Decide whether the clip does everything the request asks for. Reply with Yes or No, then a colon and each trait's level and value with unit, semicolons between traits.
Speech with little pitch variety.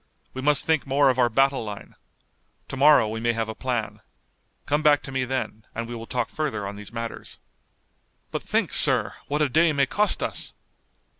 No: average, 4.0 semitones